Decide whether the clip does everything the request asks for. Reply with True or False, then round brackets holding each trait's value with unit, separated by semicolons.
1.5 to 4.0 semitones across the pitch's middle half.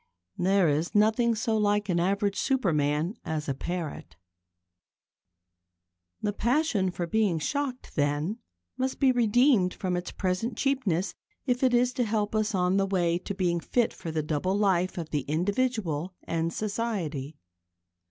False (4.9 semitones)